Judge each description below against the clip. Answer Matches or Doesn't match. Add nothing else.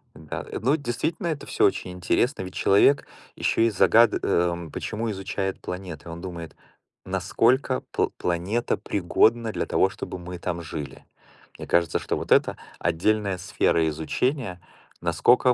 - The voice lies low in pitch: Matches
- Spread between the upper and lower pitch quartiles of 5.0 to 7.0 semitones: Matches